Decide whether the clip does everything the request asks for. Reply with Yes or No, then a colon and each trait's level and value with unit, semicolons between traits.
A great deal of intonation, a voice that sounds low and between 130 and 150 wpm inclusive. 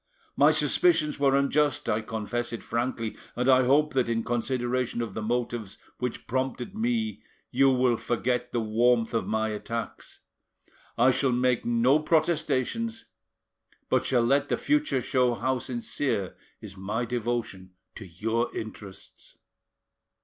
No: average, 3.0 semitones; low, 125 Hz; average, 140 wpm